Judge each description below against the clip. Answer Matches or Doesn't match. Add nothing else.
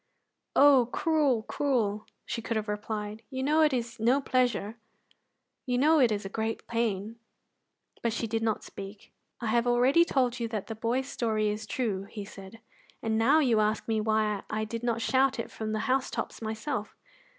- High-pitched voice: Matches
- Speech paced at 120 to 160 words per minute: Doesn't match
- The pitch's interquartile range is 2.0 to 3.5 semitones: Matches